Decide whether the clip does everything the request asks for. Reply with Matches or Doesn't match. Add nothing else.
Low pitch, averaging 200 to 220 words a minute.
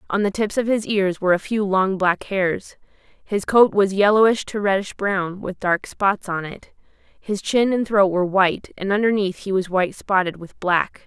Doesn't match